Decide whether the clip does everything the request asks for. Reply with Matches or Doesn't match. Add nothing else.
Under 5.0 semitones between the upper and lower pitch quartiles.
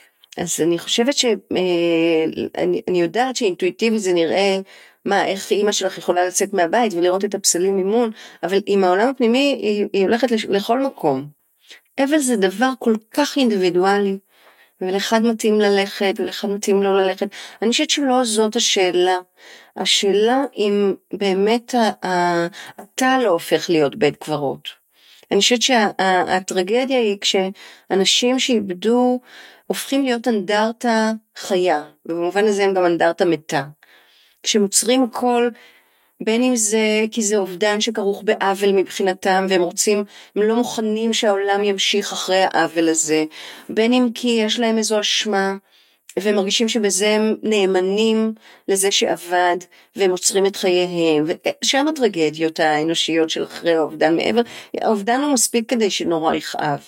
Matches